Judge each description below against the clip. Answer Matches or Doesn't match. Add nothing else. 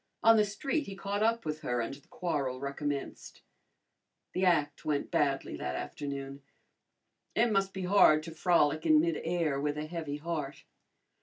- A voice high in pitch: Doesn't match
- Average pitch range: Matches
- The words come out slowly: Doesn't match